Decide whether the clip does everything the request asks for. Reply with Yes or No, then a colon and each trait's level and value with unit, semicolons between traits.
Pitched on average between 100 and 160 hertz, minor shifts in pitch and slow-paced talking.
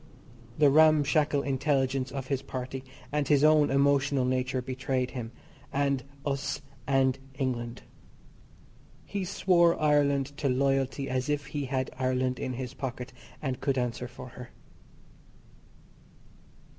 Yes: low, 135 Hz; narrow, 1.9 semitones; slow, 125 wpm